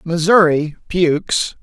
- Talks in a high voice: No, medium, 165 Hz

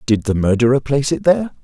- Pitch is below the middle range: Yes, low, 125 Hz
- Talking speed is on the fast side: Yes, fast, 220 wpm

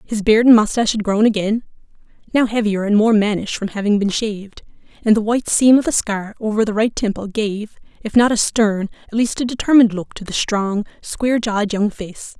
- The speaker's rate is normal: No, fast, 215 wpm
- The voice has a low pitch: No, high, 215 Hz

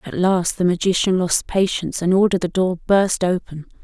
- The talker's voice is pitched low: No, medium, 185 Hz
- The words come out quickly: No, average, 190 wpm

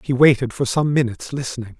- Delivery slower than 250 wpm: Yes, average, 200 wpm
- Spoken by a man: Yes, male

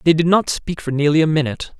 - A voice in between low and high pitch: Yes, medium, 155 Hz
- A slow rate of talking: No, fast, 265 wpm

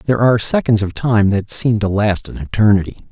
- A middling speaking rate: No, fast, 210 wpm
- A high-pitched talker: No, low, 110 Hz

